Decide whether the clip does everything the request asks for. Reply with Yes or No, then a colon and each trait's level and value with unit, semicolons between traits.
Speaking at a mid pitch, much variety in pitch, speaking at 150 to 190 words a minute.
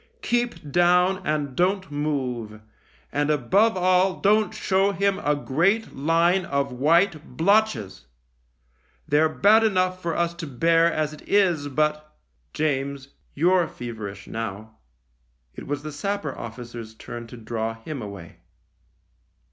No: medium, 155 Hz; wide, 6.5 semitones; slow, 135 wpm